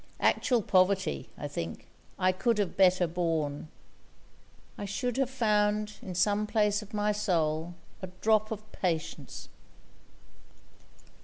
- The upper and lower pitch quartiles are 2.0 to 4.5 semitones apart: Yes, average, 3.1 semitones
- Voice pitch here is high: Yes, high, 200 Hz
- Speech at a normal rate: No, slow, 125 wpm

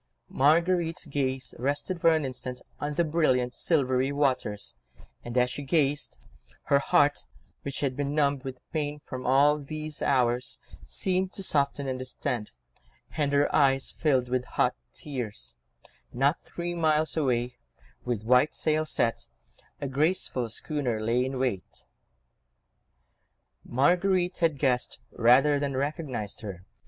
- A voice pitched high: No, medium, 140 Hz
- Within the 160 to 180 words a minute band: No, slow, 135 wpm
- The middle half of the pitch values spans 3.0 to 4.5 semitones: Yes, average, 3.3 semitones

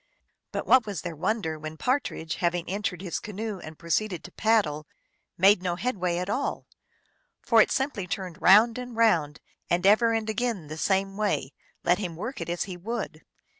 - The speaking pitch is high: Yes, high, 195 Hz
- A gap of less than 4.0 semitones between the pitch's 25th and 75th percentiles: No, average, 4.3 semitones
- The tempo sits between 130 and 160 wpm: No, average, 180 wpm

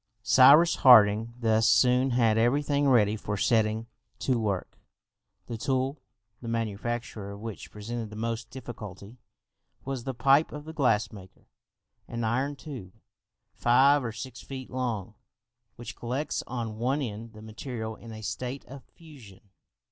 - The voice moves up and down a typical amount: Yes, average, 3.2 semitones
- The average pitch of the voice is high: No, low, 120 Hz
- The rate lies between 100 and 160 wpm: Yes, average, 150 wpm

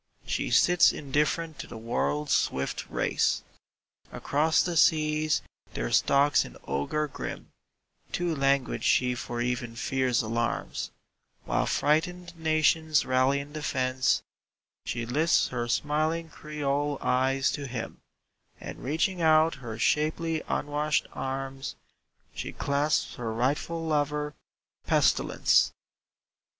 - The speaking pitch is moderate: Yes, medium, 145 Hz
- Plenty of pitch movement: No, average, 3.4 semitones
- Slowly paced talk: Yes, slow, 115 wpm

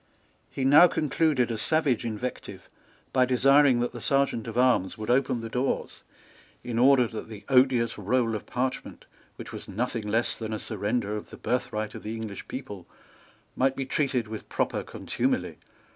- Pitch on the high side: No, low, 120 Hz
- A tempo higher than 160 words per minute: Yes, average, 170 wpm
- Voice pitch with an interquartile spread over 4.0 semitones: No, average, 3.1 semitones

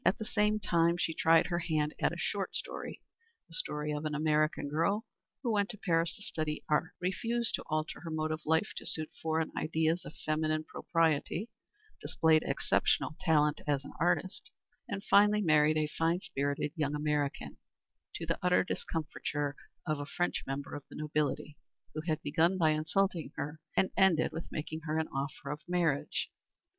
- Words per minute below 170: No, average, 175 wpm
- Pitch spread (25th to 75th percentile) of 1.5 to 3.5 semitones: Yes, narrow, 2.6 semitones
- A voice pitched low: No, medium, 160 Hz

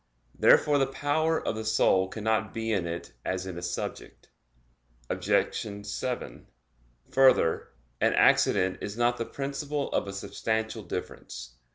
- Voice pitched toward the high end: No, low, 110 Hz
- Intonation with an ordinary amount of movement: No, wide, 6.0 semitones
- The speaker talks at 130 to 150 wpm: Yes, average, 140 wpm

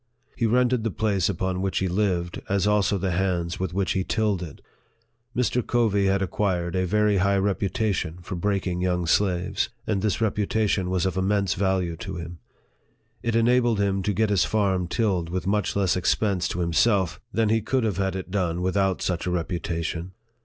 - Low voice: Yes, very low, 95 Hz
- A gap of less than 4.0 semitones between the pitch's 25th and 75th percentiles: Yes, narrow, 2.6 semitones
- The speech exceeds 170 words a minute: Yes, average, 185 wpm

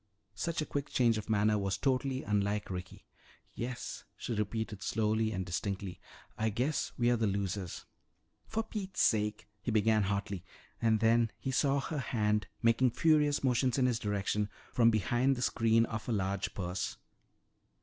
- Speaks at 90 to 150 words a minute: No, average, 165 wpm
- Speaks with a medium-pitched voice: No, low, 110 Hz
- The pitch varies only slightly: No, average, 3.6 semitones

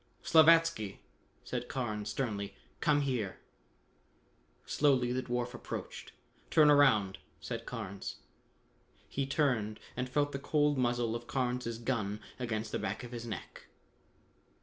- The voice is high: No, low, 125 Hz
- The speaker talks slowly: Yes, slow, 125 wpm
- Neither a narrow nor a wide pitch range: Yes, average, 4.1 semitones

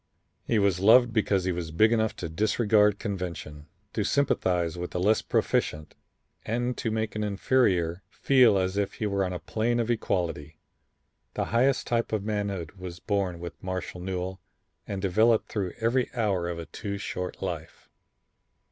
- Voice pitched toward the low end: Yes, low, 100 Hz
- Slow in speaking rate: No, average, 165 wpm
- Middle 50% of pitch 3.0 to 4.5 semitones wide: Yes, average, 3.7 semitones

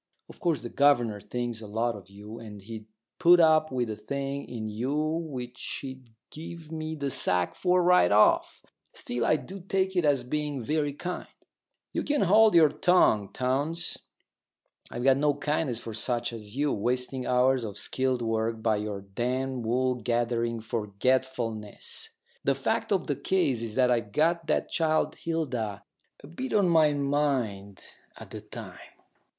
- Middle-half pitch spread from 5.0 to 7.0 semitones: Yes, wide, 5.4 semitones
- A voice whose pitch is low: Yes, low, 130 Hz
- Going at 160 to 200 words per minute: Yes, average, 165 wpm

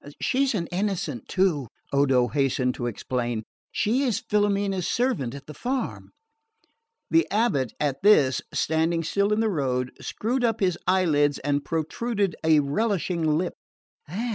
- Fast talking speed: No, average, 140 wpm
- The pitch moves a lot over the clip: Yes, wide, 6.8 semitones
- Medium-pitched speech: Yes, medium, 165 Hz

